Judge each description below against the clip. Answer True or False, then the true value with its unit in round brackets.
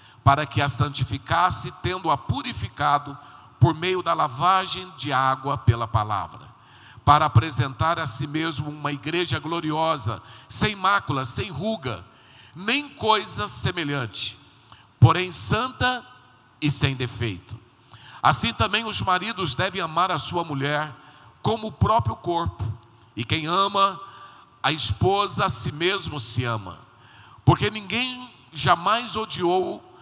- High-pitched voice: False (145 Hz)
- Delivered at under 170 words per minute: True (120 wpm)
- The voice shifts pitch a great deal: True (6.9 semitones)